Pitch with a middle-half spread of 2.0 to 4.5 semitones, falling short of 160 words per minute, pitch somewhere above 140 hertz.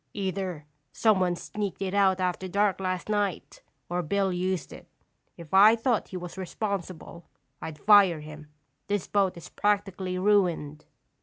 Yes: narrow, 2.4 semitones; average, 145 wpm; high, 190 Hz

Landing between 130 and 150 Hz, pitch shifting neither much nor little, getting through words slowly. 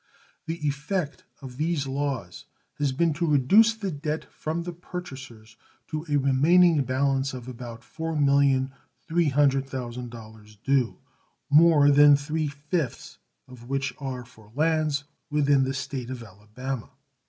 Yes: medium, 140 Hz; average, 3.2 semitones; slow, 125 wpm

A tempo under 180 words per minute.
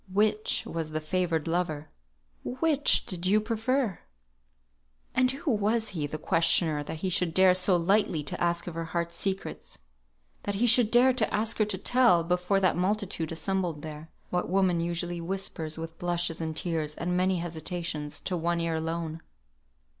Yes: average, 170 wpm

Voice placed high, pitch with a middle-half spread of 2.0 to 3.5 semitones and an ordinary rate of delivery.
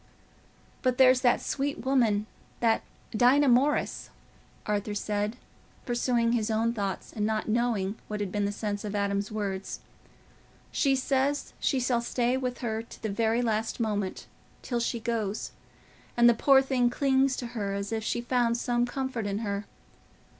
Yes: high, 230 Hz; average, 3.1 semitones; average, 155 wpm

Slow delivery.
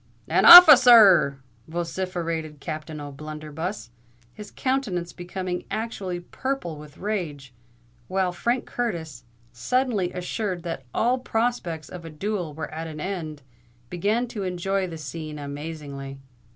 Yes: slow, 125 wpm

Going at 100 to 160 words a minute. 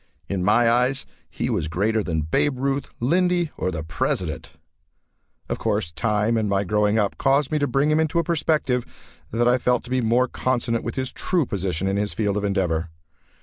No: average, 195 wpm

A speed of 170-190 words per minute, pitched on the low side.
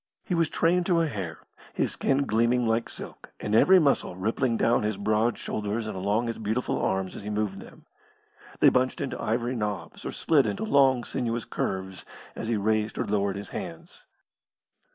Yes: average, 185 wpm; low, 115 Hz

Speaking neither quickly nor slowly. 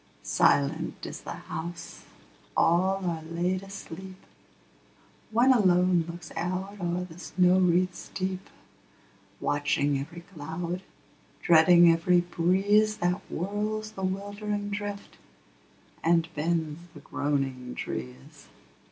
No: slow, 105 wpm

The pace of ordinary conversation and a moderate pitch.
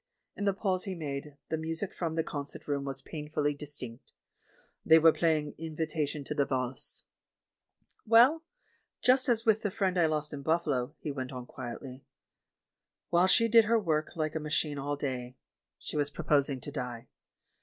Yes: average, 180 wpm; medium, 150 Hz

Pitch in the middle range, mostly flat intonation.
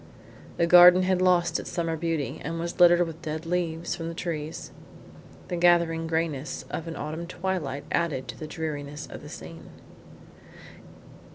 Yes: medium, 165 Hz; narrow, 1.6 semitones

